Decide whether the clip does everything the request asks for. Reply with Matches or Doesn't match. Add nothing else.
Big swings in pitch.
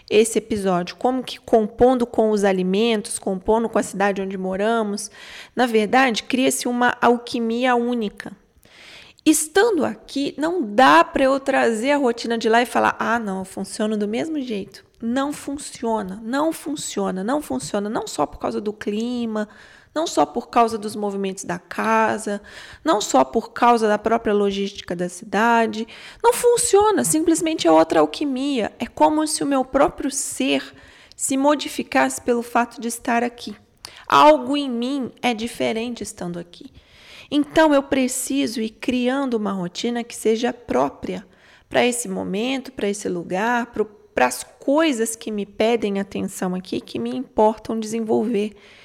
Doesn't match